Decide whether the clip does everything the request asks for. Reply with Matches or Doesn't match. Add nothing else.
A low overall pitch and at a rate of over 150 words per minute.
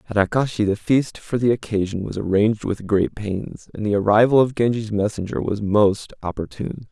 Matches